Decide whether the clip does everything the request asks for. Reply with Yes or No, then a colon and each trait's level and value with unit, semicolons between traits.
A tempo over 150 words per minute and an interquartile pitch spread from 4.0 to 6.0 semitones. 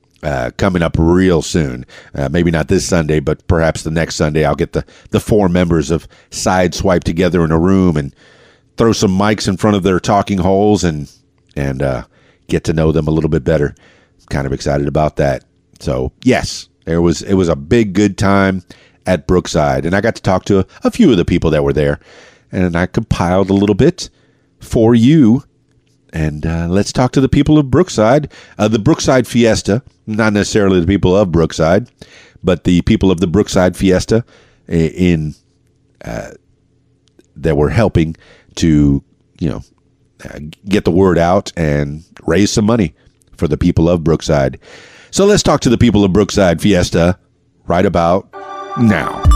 Yes: average, 180 wpm; average, 4.5 semitones